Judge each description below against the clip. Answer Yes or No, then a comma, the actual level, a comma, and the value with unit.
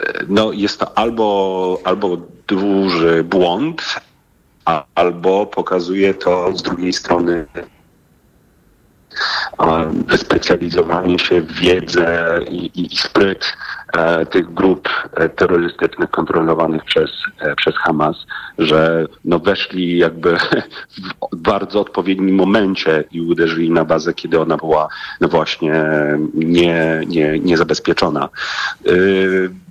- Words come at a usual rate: No, slow, 105 wpm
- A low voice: Yes, very low, 85 Hz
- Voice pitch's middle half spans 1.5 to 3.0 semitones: Yes, narrow, 2.5 semitones